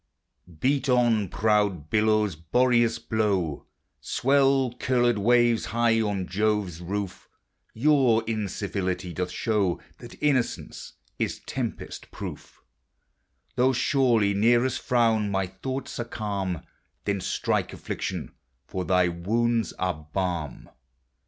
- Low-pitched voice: Yes, low, 110 Hz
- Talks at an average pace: No, slow, 105 wpm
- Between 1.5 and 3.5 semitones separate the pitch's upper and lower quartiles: No, average, 4.1 semitones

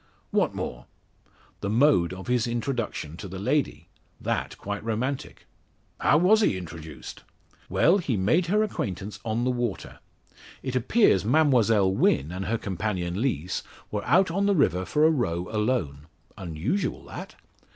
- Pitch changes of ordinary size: No, wide, 6.9 semitones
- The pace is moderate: Yes, average, 150 wpm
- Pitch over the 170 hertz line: No, low, 110 Hz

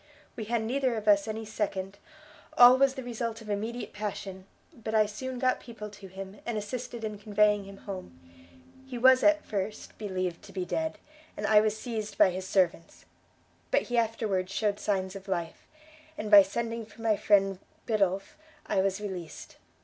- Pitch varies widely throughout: No, average, 2.8 semitones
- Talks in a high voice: Yes, high, 210 Hz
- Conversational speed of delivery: Yes, average, 180 wpm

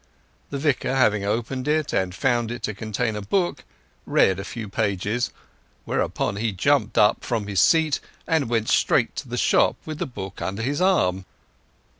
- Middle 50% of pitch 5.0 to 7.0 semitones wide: Yes, wide, 5.4 semitones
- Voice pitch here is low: Yes, low, 115 Hz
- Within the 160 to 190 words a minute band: Yes, average, 175 wpm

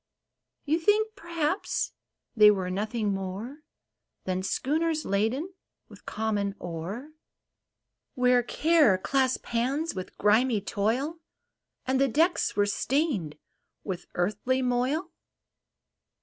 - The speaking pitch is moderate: No, high, 245 Hz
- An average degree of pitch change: No, wide, 6.9 semitones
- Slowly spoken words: Yes, slow, 105 wpm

